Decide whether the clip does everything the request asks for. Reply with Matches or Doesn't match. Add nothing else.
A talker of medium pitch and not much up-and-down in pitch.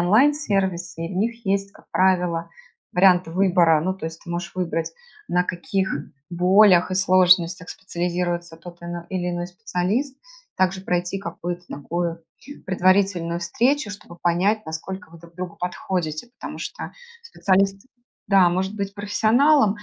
Matches